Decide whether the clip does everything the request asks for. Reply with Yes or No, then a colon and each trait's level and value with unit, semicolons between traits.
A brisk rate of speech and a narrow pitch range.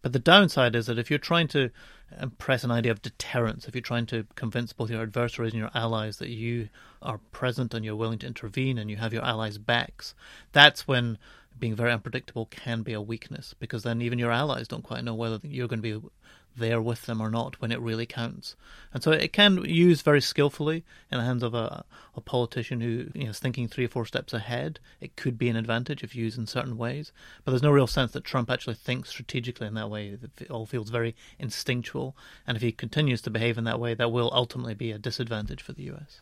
Yes: fast, 235 wpm; narrow, 2.2 semitones